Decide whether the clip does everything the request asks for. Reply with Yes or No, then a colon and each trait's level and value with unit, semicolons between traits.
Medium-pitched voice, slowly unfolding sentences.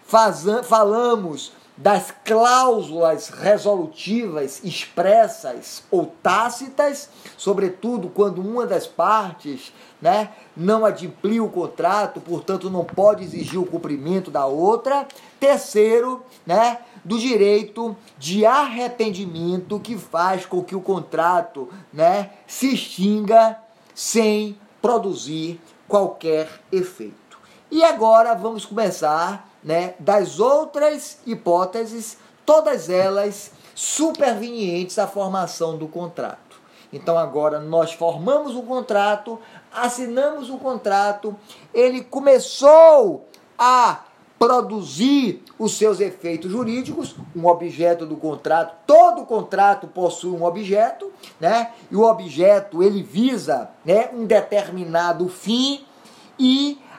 No: high, 210 Hz; slow, 105 wpm